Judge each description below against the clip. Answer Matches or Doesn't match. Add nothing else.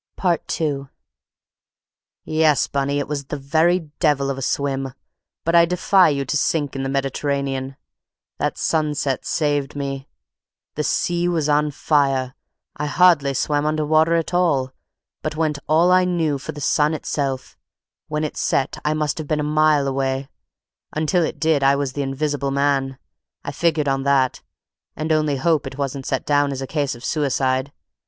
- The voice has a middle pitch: Matches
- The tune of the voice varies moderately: Doesn't match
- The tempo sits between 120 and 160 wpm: Doesn't match